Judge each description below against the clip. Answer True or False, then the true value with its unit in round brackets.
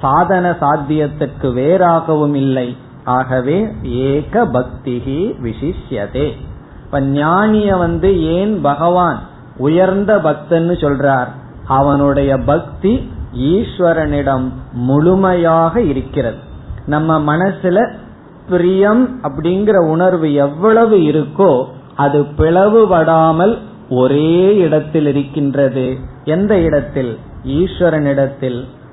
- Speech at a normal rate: False (60 wpm)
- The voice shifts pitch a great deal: False (4.7 semitones)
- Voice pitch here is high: False (150 Hz)